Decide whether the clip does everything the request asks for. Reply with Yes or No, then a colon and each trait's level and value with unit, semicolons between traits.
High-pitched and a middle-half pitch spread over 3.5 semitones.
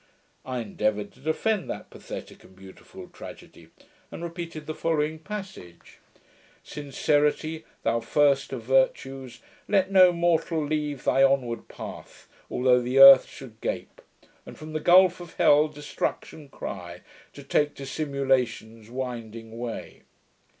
No: low, 135 Hz; average, 4.8 semitones